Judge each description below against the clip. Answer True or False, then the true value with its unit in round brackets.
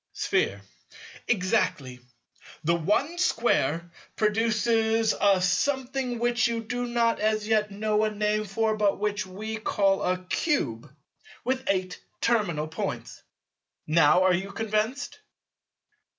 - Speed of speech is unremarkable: False (120 wpm)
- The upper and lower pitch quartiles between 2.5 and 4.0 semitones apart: True (3.7 semitones)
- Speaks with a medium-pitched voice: False (215 Hz)